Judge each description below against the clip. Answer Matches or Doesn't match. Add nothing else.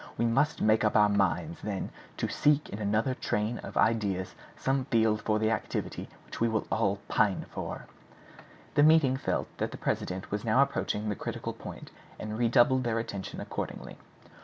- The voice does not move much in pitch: Doesn't match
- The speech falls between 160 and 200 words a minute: Matches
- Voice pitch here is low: Matches